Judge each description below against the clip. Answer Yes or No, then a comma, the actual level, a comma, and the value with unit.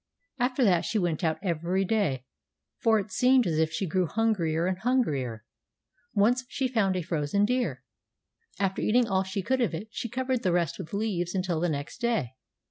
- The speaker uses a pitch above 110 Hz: Yes, high, 190 Hz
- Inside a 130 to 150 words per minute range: No, average, 190 wpm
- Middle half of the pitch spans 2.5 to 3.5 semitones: No, wide, 5.4 semitones